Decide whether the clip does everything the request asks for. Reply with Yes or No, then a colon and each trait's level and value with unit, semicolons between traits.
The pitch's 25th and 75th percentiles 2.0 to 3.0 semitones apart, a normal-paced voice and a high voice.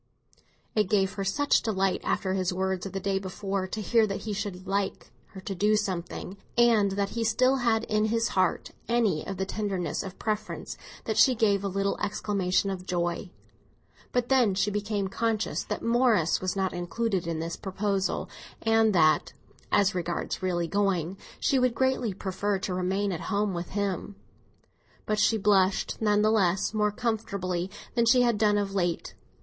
Yes: narrow, 2.5 semitones; average, 175 wpm; high, 200 Hz